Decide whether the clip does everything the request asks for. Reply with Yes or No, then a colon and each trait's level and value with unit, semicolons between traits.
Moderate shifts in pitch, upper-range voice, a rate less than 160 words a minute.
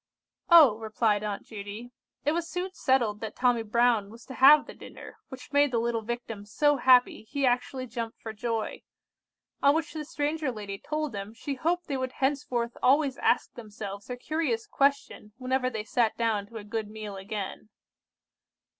No: average, 4.3 semitones; high, 240 Hz; average, 175 wpm